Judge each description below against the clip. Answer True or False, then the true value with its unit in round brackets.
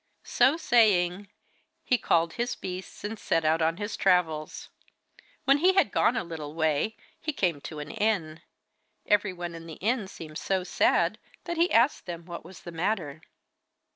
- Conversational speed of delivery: True (170 wpm)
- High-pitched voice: False (180 Hz)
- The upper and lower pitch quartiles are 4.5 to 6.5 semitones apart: True (5.2 semitones)